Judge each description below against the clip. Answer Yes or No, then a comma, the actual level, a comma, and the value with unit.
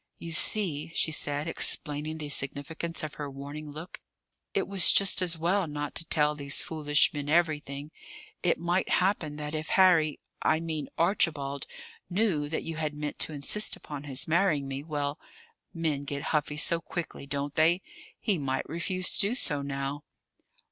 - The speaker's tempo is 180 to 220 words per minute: No, average, 170 wpm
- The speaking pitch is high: No, medium, 155 Hz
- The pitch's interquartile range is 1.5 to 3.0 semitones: Yes, average, 2.7 semitones